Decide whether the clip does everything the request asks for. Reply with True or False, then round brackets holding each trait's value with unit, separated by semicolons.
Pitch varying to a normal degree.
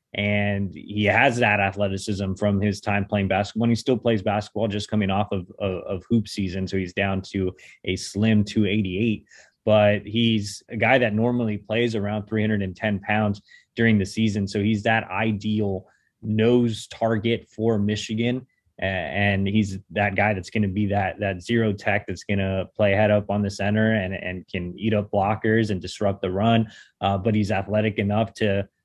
False (1.8 semitones)